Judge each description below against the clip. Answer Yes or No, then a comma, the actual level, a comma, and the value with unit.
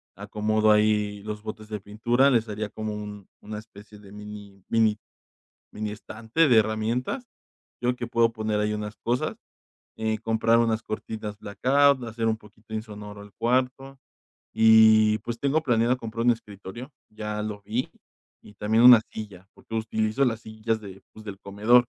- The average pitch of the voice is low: Yes, low, 110 Hz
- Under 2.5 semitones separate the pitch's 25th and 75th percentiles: Yes, narrow, 1.8 semitones